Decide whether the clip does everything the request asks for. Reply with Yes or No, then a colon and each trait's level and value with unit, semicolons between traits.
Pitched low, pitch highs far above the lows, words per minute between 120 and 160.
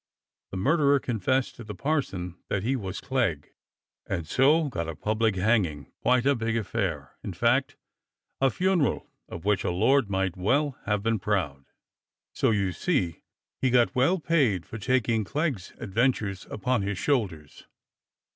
Yes: low, 110 Hz; wide, 5.9 semitones; average, 155 wpm